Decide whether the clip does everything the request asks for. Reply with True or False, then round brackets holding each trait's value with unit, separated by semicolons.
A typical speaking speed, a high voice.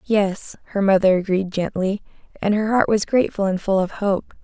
True (190 wpm; 200 Hz)